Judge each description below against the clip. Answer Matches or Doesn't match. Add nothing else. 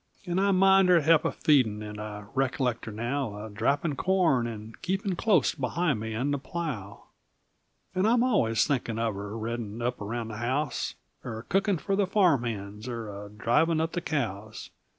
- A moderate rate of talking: Matches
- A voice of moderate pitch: Doesn't match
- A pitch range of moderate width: Doesn't match